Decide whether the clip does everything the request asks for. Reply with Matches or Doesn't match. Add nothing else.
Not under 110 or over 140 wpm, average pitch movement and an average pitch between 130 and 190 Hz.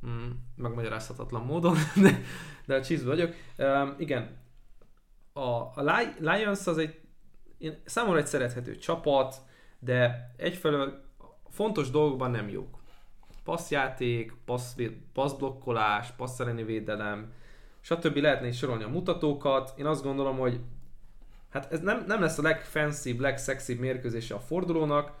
Matches